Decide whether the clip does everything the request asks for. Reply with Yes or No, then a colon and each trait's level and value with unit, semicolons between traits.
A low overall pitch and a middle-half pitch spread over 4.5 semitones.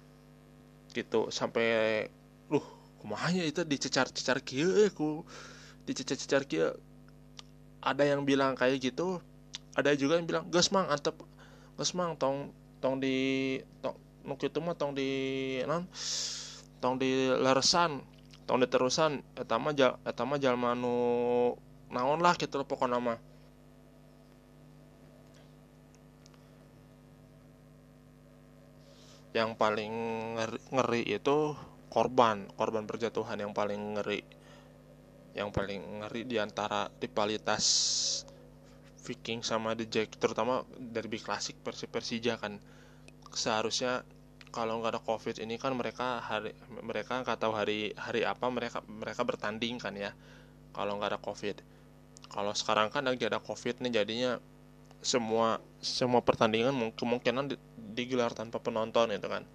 No: low, 120 Hz; average, 3.5 semitones